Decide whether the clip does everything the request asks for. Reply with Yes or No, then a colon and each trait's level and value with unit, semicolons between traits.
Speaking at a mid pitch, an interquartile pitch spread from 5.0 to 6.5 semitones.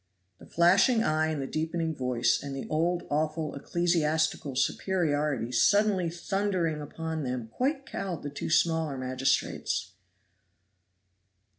No: medium, 160 Hz; average, 3.7 semitones